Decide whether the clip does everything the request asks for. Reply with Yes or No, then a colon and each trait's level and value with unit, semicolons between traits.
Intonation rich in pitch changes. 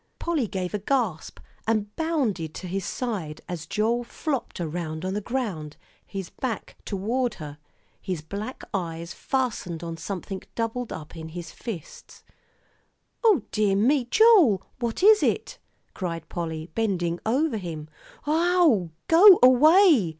Yes: wide, 7.2 semitones